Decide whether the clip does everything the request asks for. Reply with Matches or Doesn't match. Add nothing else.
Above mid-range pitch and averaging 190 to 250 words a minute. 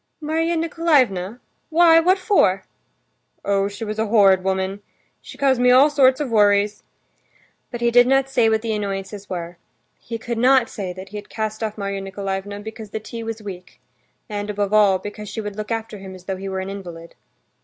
Matches